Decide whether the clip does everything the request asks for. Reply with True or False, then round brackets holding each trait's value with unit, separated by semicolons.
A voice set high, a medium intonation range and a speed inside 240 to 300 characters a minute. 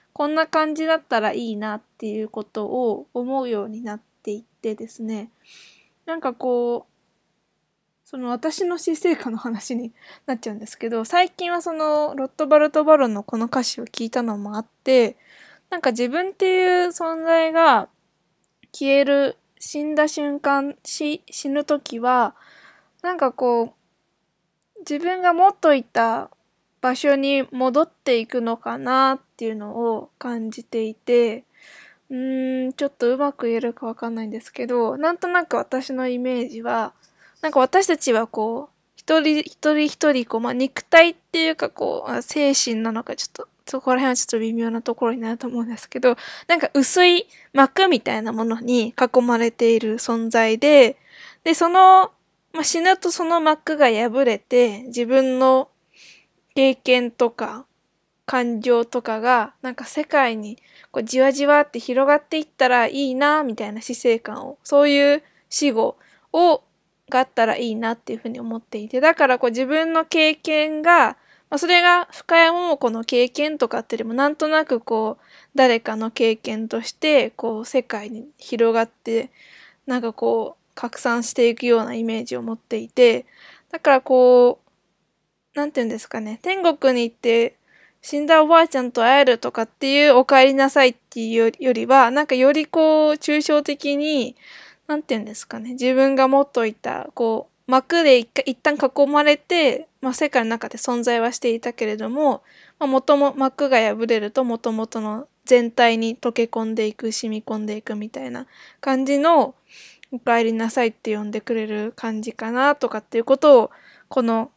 False (255 Hz; 4.3 semitones; 320 characters per minute)